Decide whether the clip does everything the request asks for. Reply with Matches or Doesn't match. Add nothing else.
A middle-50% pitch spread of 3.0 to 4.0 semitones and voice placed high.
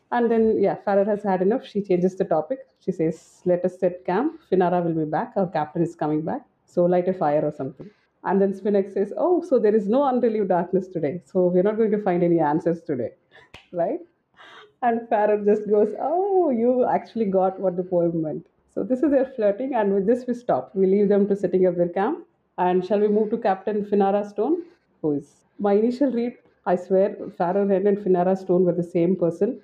Matches